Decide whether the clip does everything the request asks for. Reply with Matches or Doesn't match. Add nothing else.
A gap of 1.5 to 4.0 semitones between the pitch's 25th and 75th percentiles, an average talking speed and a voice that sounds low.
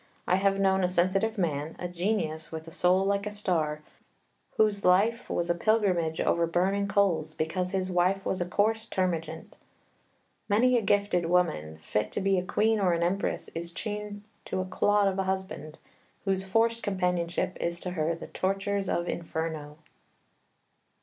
Doesn't match